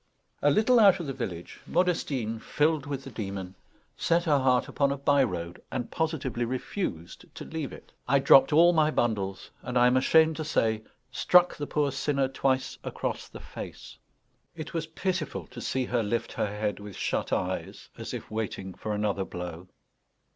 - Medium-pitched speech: No, low, 130 Hz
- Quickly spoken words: No, average, 180 wpm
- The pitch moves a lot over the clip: Yes, wide, 6.2 semitones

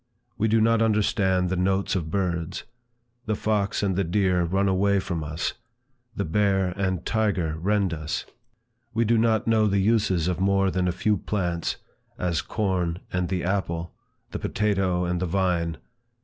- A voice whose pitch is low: Yes, very low, 95 Hz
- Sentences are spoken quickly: No, average, 165 wpm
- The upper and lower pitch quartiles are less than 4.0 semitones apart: Yes, average, 2.7 semitones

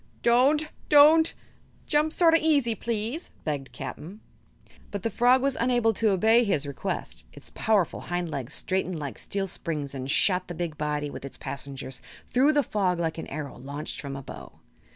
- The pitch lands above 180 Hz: Yes, high, 190 Hz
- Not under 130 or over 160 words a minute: No, average, 180 wpm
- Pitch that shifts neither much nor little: No, wide, 8.7 semitones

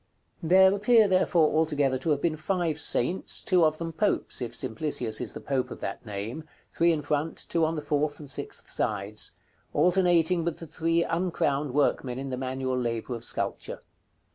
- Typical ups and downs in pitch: Yes, average, 4.4 semitones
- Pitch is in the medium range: Yes, medium, 155 Hz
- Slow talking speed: No, average, 180 wpm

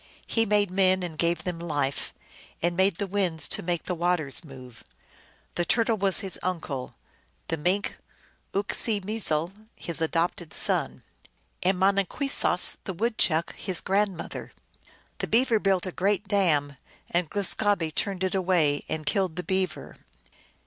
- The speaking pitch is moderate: Yes, medium, 180 Hz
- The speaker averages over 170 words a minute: No, average, 150 wpm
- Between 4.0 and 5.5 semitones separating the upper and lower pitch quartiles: No, average, 3.2 semitones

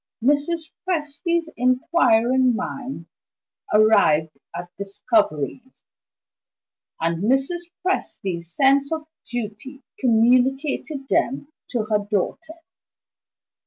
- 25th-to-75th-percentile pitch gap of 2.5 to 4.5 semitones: No, average, 5.3 semitones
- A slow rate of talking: Yes, slow, 80 wpm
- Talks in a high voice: Yes, very high, 255 Hz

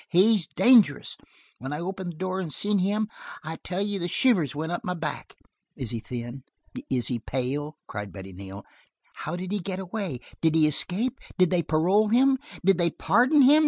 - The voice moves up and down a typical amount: No, wide, 5.7 semitones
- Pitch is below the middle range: No, medium, 175 Hz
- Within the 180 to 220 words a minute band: Yes, average, 195 wpm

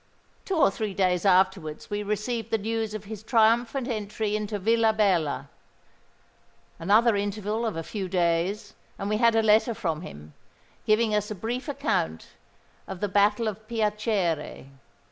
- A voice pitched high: Yes, high, 210 Hz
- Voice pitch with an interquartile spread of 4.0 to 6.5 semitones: No, average, 2.8 semitones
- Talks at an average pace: Yes, average, 145 wpm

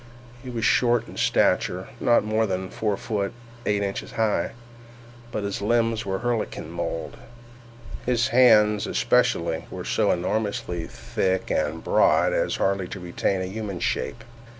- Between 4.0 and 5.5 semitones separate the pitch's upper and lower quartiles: No, average, 3.3 semitones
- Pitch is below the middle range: Yes, low, 105 Hz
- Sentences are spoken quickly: No, average, 150 wpm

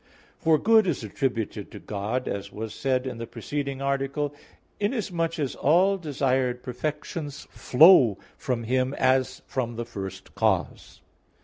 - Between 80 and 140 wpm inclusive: Yes, slow, 135 wpm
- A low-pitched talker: Yes, low, 130 Hz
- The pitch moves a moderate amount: Yes, average, 4.2 semitones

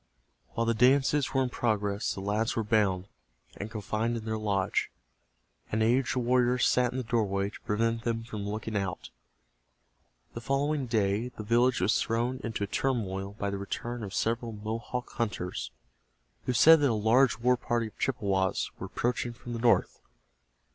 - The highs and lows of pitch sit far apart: No, average, 2.8 semitones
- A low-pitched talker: Yes, low, 115 Hz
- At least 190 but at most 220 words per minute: No, average, 170 wpm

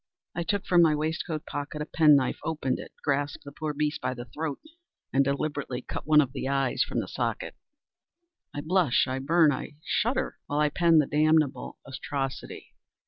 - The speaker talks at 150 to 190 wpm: Yes, average, 185 wpm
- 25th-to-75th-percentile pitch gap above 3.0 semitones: No, narrow, 2.4 semitones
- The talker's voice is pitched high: No, medium, 150 Hz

